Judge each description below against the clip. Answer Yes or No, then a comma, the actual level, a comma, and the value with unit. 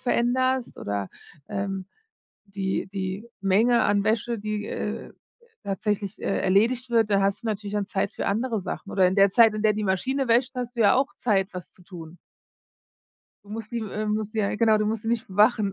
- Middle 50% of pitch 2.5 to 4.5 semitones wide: Yes, average, 2.8 semitones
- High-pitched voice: Yes, high, 210 Hz